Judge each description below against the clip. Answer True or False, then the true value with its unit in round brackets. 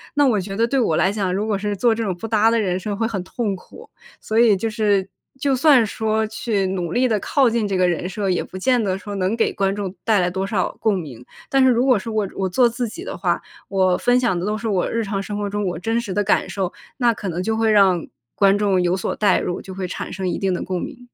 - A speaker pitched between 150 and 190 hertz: False (205 Hz)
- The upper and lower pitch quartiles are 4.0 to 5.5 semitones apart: False (3.2 semitones)